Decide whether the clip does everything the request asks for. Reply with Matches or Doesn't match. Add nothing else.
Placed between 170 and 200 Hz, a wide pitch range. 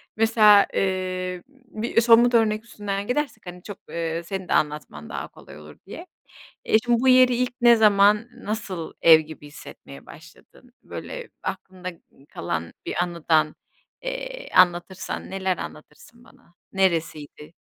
Matches